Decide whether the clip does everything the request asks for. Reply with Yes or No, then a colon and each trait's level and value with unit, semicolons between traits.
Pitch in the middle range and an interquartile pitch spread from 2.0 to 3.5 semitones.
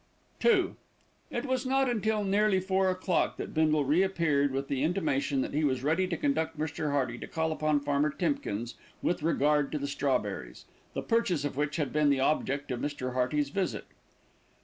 No: medium, 150 Hz; average, 4.9 semitones